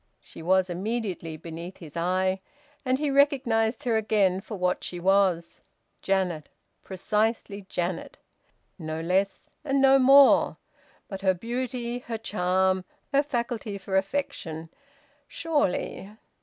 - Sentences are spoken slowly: Yes, slow, 120 wpm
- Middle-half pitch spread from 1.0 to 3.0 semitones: No, average, 4.8 semitones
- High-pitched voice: Yes, high, 195 Hz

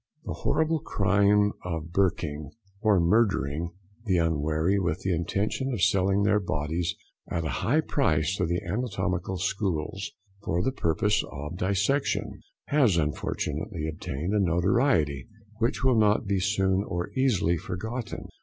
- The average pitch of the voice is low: Yes, very low, 95 Hz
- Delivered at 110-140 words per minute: Yes, slow, 135 wpm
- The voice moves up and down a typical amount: Yes, average, 4.2 semitones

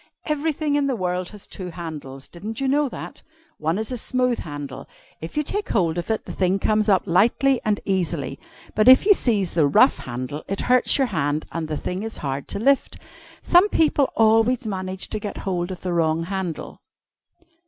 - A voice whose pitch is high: Yes, high, 195 Hz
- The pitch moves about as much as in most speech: No, wide, 7.0 semitones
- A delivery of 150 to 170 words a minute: No, average, 195 wpm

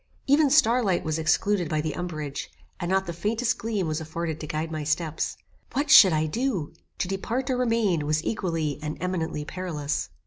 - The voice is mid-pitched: Yes, medium, 170 Hz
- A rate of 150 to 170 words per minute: No, average, 185 wpm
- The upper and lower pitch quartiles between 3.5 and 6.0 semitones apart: Yes, wide, 5.6 semitones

